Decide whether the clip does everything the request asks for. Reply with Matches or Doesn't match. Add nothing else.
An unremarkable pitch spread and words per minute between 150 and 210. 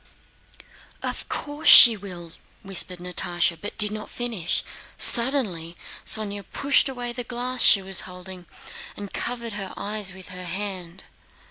Doesn't match